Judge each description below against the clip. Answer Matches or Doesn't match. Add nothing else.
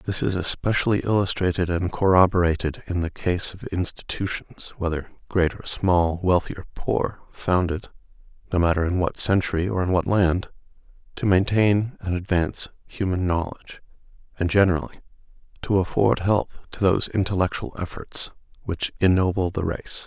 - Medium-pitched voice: Doesn't match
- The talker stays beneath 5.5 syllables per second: Matches